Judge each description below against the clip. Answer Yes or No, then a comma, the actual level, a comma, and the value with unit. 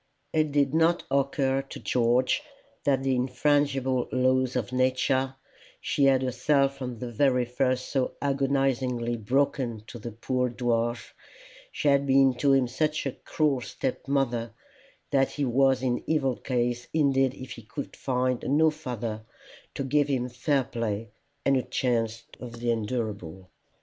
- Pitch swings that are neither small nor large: No, narrow, 2.2 semitones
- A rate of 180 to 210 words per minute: No, average, 150 wpm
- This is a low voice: Yes, low, 130 Hz